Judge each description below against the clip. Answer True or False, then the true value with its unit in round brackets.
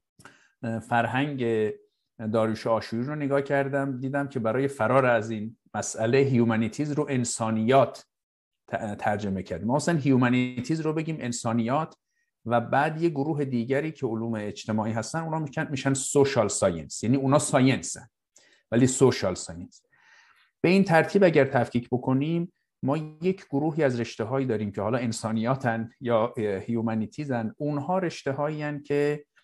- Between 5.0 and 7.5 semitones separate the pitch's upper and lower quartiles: False (4.4 semitones)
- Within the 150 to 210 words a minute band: False (135 wpm)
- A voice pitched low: True (130 Hz)